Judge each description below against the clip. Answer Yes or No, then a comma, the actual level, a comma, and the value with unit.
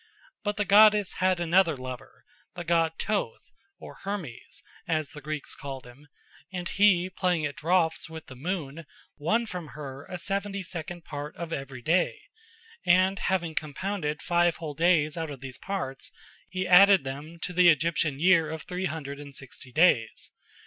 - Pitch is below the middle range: No, medium, 165 Hz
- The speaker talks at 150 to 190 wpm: Yes, average, 165 wpm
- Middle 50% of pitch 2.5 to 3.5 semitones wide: No, average, 4.1 semitones